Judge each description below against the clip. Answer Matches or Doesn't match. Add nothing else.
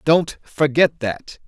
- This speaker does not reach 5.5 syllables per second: Matches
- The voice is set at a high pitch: Doesn't match